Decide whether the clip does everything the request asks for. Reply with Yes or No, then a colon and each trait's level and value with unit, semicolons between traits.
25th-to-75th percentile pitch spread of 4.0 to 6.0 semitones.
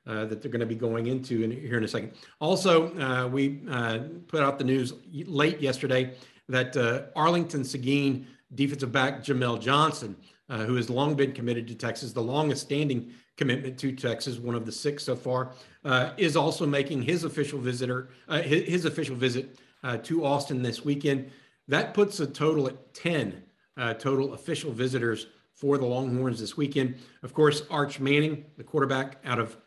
No: average, 2.7 semitones